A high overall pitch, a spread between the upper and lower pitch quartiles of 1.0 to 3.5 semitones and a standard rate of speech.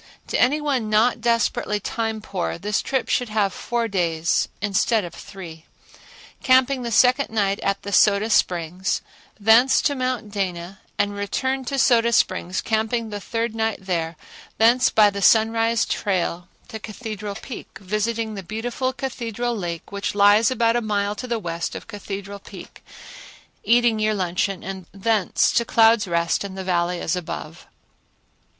Yes: high, 215 Hz; average, 3.2 semitones; average, 160 wpm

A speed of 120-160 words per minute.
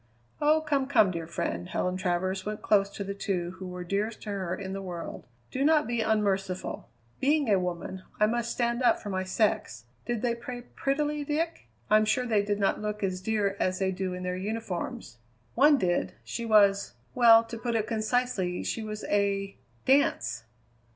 No: average, 190 wpm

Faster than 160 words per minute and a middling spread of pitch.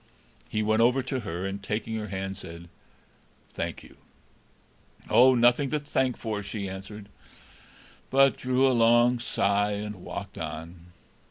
No: average, 145 wpm; average, 4.2 semitones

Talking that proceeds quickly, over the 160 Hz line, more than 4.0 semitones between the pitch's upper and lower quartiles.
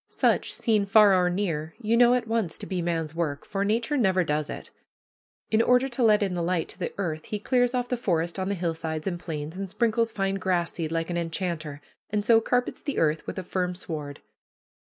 Yes: fast, 225 wpm; medium, 185 Hz; average, 5.1 semitones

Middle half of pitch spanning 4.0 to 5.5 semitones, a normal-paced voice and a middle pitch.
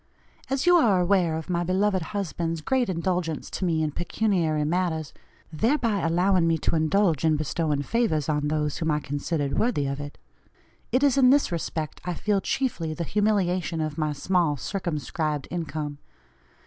Yes: average, 4.3 semitones; average, 165 wpm; medium, 170 Hz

